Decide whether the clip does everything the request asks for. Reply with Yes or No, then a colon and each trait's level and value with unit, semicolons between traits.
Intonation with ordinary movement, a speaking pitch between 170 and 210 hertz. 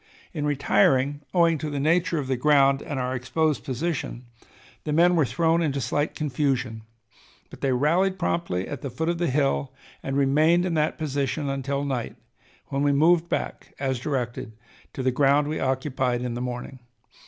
No: average, 3.1 semitones; medium, 140 Hz